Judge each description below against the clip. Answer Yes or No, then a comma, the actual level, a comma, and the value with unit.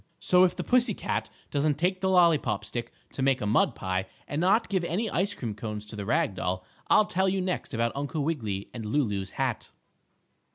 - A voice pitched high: No, medium, 140 Hz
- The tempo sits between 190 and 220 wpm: Yes, fast, 205 wpm